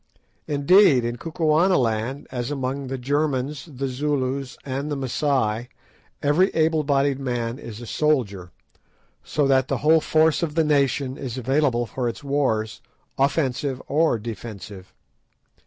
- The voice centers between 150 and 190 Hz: No, low, 135 Hz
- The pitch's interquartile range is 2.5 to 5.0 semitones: Yes, average, 3.3 semitones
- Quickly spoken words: No, slow, 135 wpm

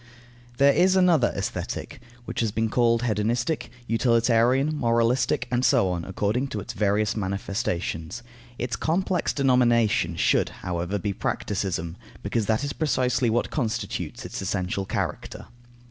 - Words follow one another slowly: Yes, slow, 130 wpm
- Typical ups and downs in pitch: Yes, average, 4.0 semitones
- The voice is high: No, low, 115 Hz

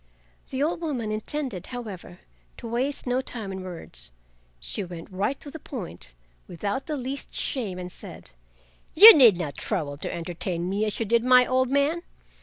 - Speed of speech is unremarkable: Yes, average, 175 wpm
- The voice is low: No, high, 225 Hz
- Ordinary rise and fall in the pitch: No, wide, 6.6 semitones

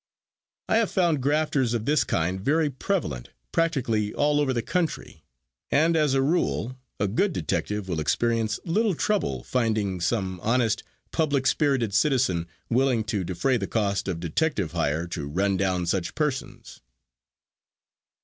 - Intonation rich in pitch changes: Yes, wide, 7.6 semitones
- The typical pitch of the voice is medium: No, low, 120 Hz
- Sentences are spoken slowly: No, average, 145 wpm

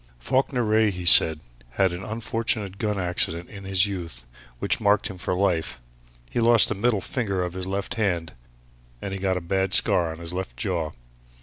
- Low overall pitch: Yes, very low, 95 Hz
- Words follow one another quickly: No, average, 190 wpm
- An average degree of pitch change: Yes, average, 3.1 semitones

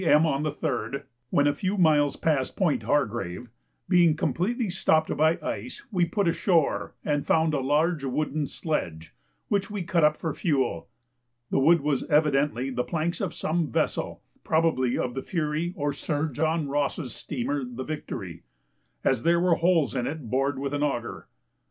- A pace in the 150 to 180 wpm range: Yes, average, 170 wpm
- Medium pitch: Yes, medium, 150 Hz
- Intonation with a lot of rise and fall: No, average, 3.2 semitones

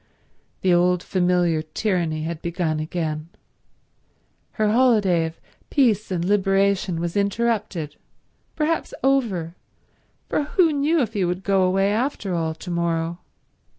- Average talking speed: No, slow, 120 wpm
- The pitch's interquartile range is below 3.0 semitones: No, average, 4.1 semitones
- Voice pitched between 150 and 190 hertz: Yes, medium, 185 Hz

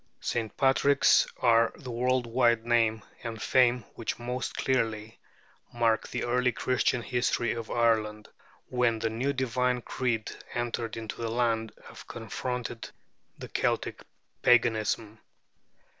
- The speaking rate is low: Yes, slow, 125 wpm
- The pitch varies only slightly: Yes, narrow, 1.8 semitones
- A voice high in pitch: No, low, 120 Hz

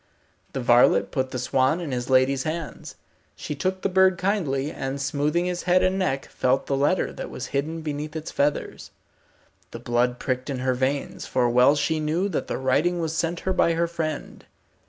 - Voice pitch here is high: No, medium, 145 Hz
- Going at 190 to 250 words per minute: Yes, average, 195 wpm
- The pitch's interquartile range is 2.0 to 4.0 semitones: No, average, 4.5 semitones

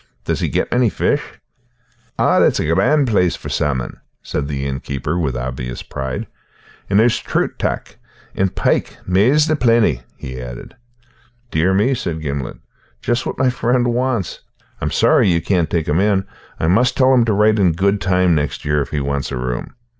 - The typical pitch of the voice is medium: No, very low, 90 Hz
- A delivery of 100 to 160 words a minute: No, average, 185 wpm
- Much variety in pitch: Yes, wide, 8.4 semitones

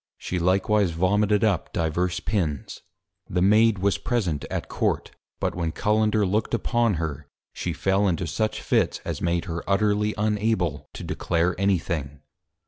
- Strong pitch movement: No, average, 3.8 semitones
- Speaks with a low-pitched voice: Yes, very low, 95 Hz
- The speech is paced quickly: No, average, 155 wpm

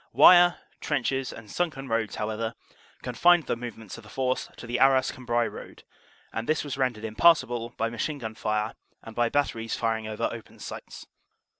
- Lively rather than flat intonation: No, average, 3.1 semitones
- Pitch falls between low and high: No, low, 120 Hz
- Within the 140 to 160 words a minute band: No, average, 175 wpm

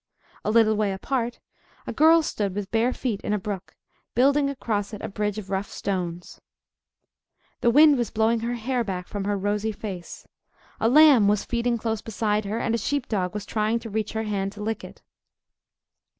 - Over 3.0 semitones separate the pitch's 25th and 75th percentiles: No, narrow, 2.6 semitones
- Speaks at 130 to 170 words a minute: No, average, 190 wpm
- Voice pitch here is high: Yes, high, 215 Hz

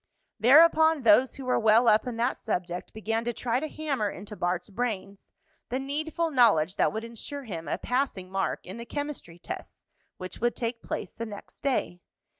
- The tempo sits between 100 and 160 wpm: No, average, 185 wpm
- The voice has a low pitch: No, high, 230 Hz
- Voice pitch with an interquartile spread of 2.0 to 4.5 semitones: No, average, 4.9 semitones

